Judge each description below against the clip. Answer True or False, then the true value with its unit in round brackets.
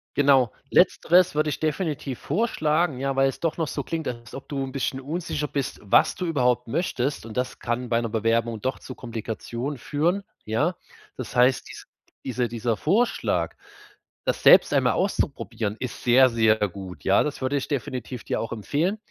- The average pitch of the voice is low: True (130 Hz)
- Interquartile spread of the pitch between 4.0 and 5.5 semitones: True (4.3 semitones)